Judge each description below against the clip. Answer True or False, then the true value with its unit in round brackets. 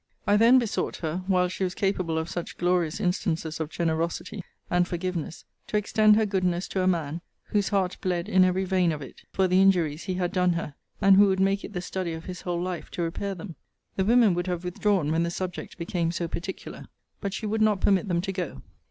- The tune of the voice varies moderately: False (2.2 semitones)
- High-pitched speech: False (180 Hz)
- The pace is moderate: False (225 wpm)